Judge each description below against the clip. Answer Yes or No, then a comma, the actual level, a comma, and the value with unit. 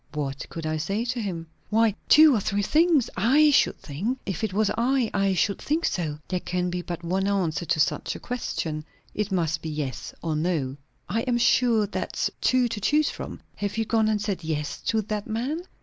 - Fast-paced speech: Yes, fast, 210 wpm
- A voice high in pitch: Yes, high, 200 Hz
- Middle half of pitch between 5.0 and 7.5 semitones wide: Yes, wide, 5.6 semitones